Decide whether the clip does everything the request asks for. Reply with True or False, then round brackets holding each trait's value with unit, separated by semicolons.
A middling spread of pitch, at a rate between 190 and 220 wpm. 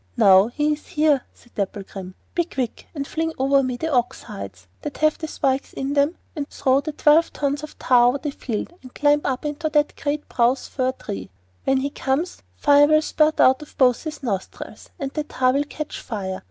True (3.2 semitones; 205 wpm)